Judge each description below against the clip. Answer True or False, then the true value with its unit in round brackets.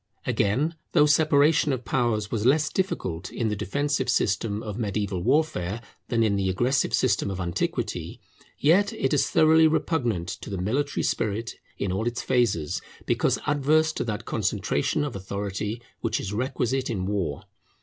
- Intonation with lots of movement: True (6.4 semitones)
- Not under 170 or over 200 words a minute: False (160 wpm)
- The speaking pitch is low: True (115 Hz)